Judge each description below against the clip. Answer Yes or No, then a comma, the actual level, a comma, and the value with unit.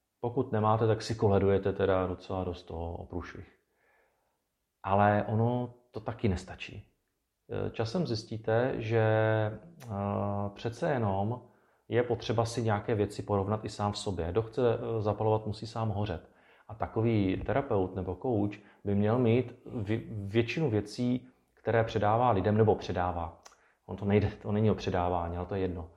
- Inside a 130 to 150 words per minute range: Yes, average, 145 wpm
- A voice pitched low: Yes, low, 105 Hz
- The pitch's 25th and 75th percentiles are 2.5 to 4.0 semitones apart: Yes, average, 2.8 semitones